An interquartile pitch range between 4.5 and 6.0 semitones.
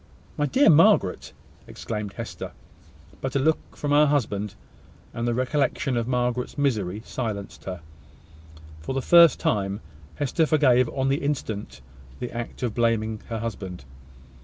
Yes: average, 5.1 semitones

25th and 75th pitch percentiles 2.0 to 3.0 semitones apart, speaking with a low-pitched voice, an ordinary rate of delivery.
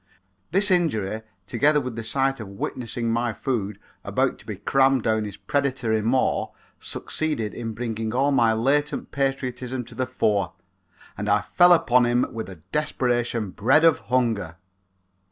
No: average, 3.5 semitones; low, 120 Hz; average, 155 wpm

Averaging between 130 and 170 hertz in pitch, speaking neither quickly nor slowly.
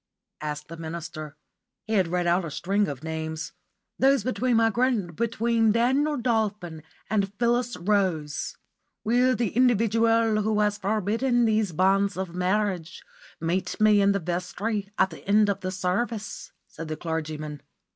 No: high, 200 Hz; average, 150 wpm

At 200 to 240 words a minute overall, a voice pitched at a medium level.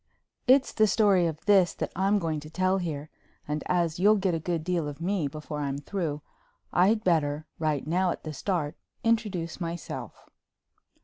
No: average, 175 wpm; medium, 170 Hz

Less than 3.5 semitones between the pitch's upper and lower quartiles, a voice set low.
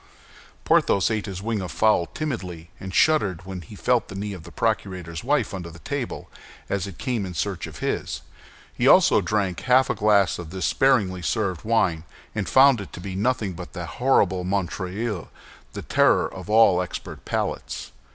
No: average, 3.8 semitones; low, 100 Hz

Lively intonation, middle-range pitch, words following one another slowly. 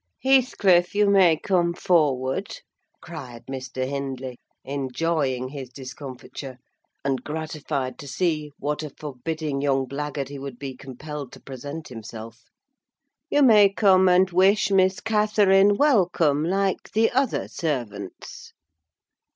Yes: wide, 6.0 semitones; medium, 150 Hz; slow, 120 wpm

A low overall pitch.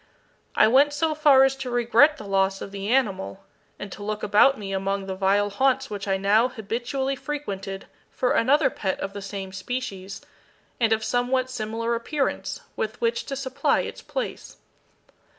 No: high, 225 Hz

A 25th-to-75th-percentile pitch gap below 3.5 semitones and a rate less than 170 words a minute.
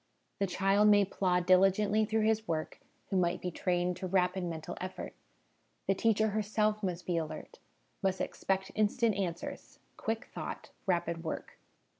Yes: average, 2.9 semitones; average, 145 wpm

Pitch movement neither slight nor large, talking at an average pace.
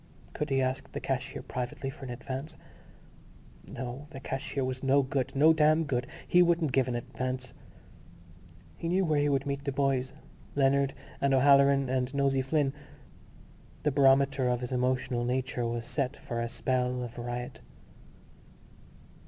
No: narrow, 1.8 semitones; average, 155 wpm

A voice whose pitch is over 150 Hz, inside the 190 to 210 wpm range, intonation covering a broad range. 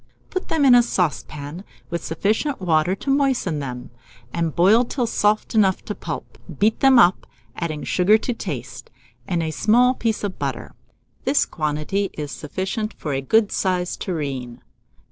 No: medium, 185 Hz; average, 160 wpm; wide, 6.4 semitones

